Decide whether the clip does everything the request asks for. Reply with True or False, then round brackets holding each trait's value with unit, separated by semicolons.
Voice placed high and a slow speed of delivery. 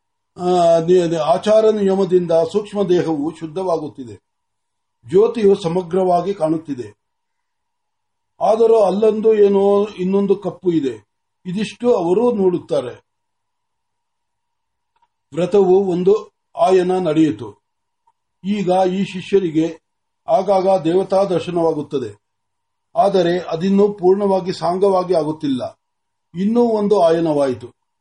True (195 Hz; 75 wpm)